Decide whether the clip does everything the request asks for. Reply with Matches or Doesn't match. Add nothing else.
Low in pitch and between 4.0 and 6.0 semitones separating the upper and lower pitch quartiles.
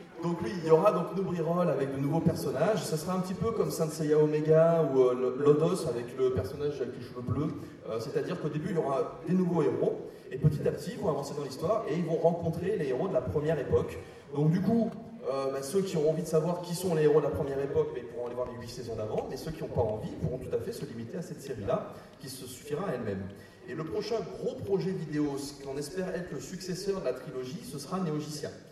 Doesn't match